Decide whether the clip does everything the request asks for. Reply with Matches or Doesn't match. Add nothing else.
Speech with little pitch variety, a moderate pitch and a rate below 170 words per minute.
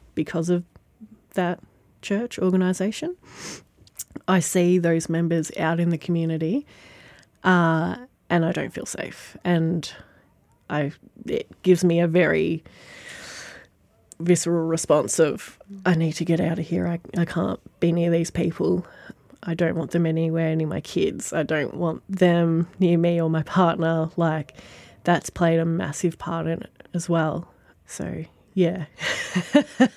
Matches